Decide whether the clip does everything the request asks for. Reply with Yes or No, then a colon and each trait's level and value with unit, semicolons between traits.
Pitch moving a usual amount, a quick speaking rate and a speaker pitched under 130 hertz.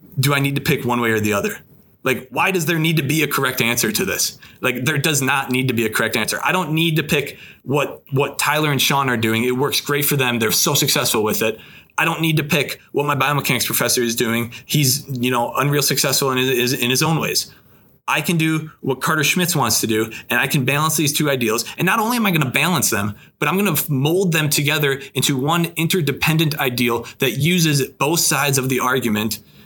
No: average, 3.9 semitones; fast, 245 wpm; medium, 140 Hz